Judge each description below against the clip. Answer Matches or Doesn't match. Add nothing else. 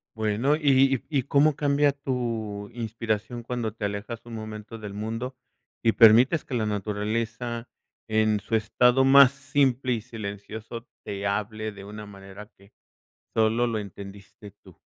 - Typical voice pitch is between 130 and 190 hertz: Doesn't match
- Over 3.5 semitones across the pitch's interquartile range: Doesn't match